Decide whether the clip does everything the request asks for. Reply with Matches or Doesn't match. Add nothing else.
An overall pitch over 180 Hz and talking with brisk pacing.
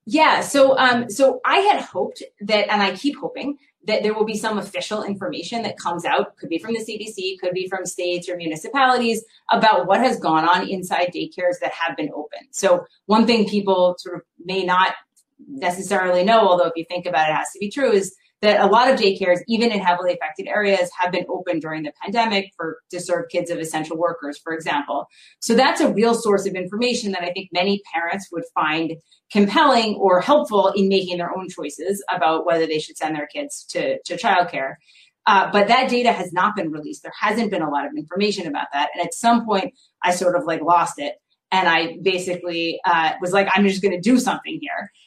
Matches